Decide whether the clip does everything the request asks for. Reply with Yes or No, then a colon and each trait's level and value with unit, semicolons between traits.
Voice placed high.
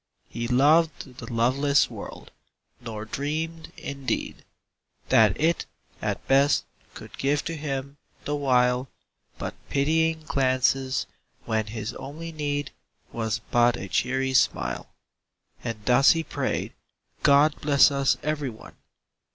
No: low, 135 Hz